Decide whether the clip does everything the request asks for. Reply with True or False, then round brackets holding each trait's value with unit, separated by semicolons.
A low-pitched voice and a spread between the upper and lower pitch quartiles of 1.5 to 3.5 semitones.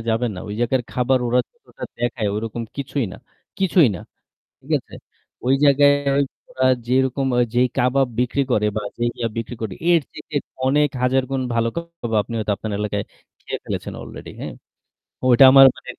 True (125 Hz; 2.9 semitones)